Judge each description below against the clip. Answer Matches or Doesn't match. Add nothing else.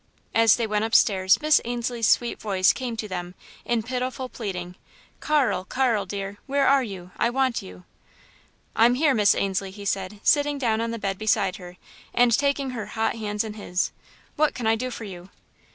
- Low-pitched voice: Doesn't match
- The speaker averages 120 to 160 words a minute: Doesn't match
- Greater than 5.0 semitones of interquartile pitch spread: Doesn't match